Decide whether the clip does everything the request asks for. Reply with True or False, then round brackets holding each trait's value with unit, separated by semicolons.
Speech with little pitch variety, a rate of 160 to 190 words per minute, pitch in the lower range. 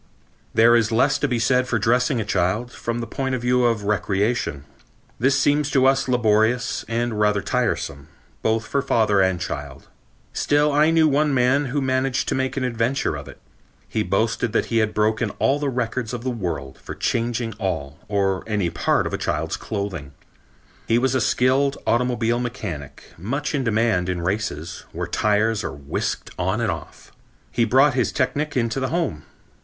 False (4.2 semitones; 180 wpm; 115 Hz)